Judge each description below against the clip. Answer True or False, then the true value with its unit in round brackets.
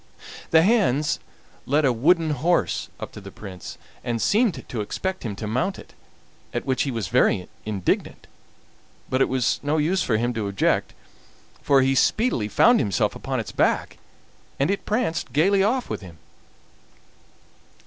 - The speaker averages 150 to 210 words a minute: True (160 wpm)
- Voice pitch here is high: False (135 Hz)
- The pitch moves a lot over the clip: True (8.3 semitones)